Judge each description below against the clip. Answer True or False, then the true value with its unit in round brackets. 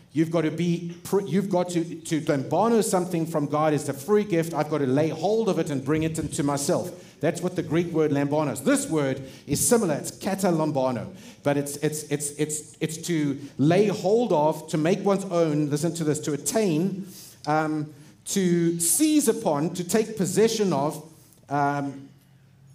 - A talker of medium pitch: True (160 Hz)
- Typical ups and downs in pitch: True (3.4 semitones)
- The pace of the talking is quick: False (180 wpm)